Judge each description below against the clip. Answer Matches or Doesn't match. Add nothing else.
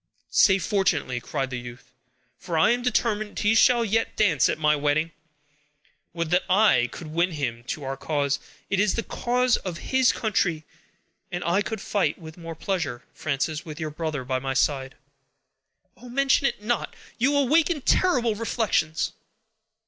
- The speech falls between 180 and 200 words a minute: Doesn't match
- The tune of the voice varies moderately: Doesn't match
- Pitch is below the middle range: Doesn't match